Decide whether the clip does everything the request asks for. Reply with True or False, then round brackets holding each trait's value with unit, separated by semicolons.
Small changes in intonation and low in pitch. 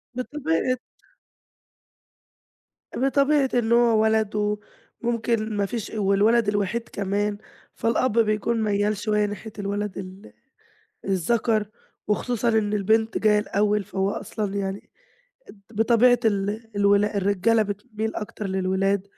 False (2.1 semitones; 210 Hz)